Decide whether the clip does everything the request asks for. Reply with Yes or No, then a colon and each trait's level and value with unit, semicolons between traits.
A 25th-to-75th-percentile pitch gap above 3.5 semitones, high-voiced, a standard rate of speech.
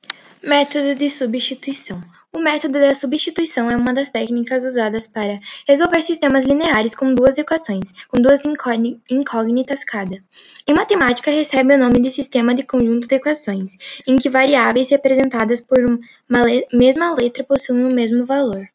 No: average, 2.8 semitones; very high, 260 Hz; average, 150 wpm